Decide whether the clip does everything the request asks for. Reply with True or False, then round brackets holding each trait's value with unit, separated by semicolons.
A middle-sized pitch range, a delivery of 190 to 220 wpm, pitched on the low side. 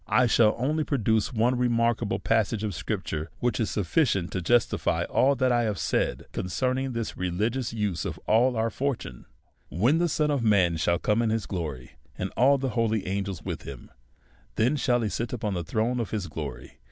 True (4.4 semitones; 195 wpm; 110 Hz)